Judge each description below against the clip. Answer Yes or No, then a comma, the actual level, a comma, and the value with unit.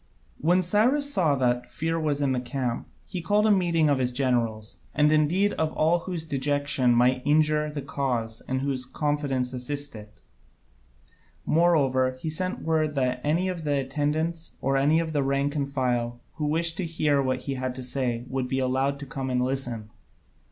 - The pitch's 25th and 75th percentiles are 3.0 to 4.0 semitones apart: Yes, average, 3.6 semitones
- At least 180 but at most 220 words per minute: Yes, average, 185 wpm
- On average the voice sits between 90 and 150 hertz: Yes, medium, 140 Hz